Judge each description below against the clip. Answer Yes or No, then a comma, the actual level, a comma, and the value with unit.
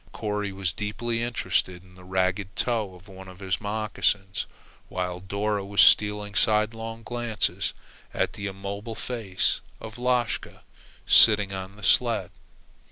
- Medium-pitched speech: No, low, 105 Hz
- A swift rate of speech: No, slow, 135 wpm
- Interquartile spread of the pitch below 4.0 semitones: Yes, narrow, 2.6 semitones